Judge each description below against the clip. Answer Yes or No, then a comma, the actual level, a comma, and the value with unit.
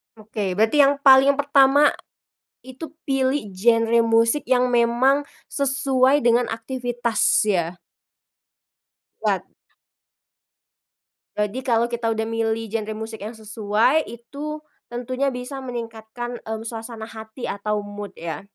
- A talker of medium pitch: No, high, 235 Hz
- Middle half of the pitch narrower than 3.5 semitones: Yes, average, 3.1 semitones